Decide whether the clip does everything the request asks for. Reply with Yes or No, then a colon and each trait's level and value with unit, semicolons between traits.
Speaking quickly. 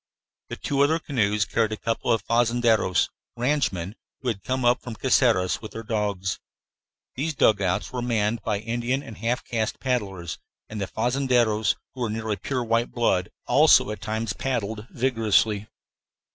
No: average, 160 wpm